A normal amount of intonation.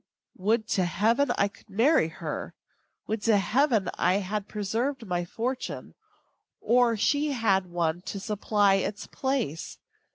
Yes: average, 3.9 semitones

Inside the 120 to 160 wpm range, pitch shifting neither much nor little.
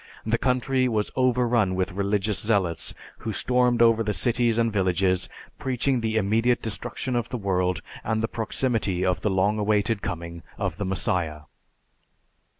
Yes: average, 155 wpm; average, 3.8 semitones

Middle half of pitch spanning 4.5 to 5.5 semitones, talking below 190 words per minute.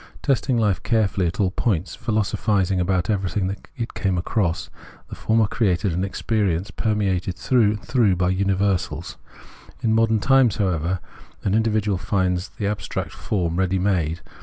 No: average, 3.0 semitones; average, 145 wpm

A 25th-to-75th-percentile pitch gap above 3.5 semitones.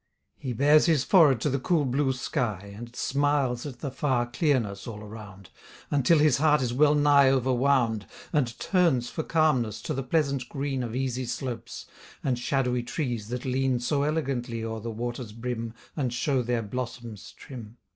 No: average, 3.2 semitones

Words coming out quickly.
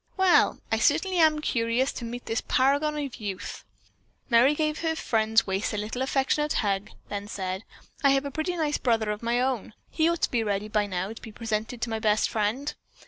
Yes: fast, 210 wpm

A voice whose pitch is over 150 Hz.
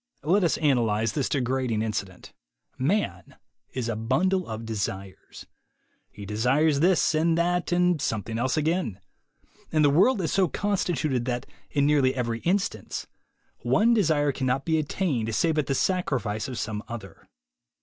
No: medium, 140 Hz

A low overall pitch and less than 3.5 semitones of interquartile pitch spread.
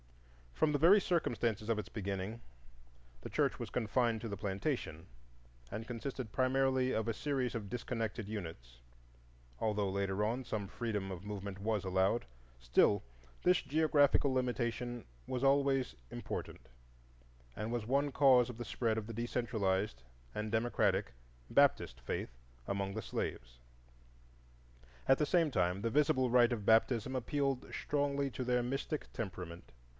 No: low, 115 Hz; average, 4.4 semitones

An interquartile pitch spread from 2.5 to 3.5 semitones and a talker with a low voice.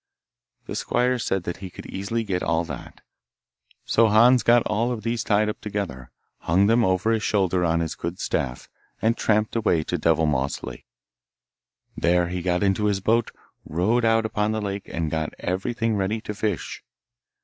No: average, 4.3 semitones; low, 100 Hz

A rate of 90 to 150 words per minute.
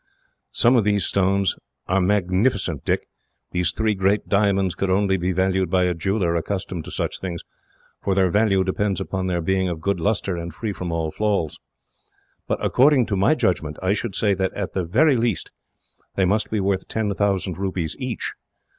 No: average, 185 wpm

